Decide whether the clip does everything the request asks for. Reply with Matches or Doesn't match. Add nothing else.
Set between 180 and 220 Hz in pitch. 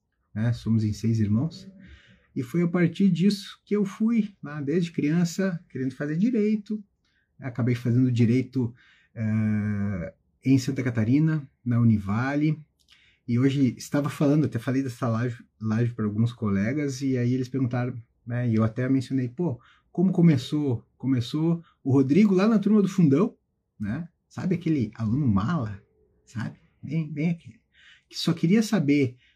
Doesn't match